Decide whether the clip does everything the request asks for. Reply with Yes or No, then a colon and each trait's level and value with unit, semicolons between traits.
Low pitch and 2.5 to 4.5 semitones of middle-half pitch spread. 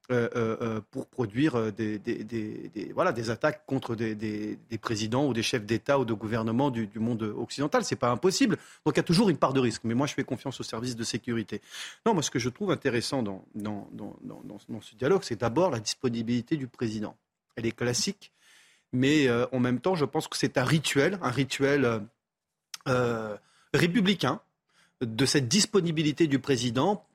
Yes: low, 125 Hz; average, 4.1 semitones